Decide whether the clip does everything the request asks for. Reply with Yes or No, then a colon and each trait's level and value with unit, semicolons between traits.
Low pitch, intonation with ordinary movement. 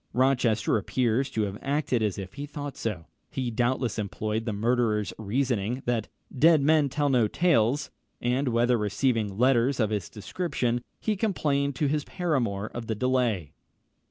Yes: low, 120 Hz; average, 4.2 semitones